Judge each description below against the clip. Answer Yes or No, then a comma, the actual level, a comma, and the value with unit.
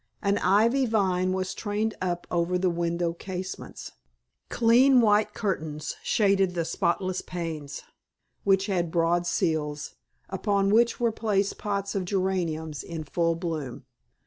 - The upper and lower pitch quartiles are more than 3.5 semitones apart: No, average, 3.2 semitones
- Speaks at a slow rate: Yes, slow, 130 wpm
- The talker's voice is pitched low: No, medium, 185 Hz